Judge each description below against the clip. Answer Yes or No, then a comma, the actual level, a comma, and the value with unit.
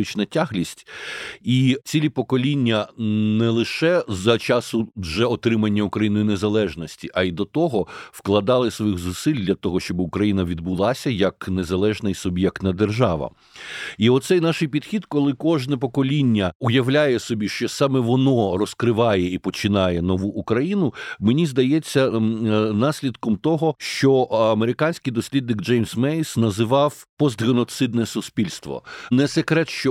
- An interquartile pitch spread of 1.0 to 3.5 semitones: No, average, 4.8 semitones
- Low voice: Yes, low, 115 Hz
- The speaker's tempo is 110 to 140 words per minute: Yes, average, 120 wpm